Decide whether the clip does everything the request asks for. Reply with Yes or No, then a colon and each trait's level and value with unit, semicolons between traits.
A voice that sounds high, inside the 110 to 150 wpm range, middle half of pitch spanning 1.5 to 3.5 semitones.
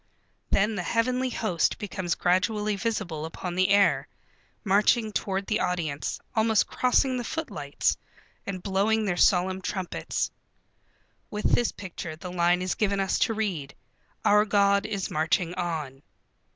Yes: high, 195 Hz; average, 140 wpm; average, 3.2 semitones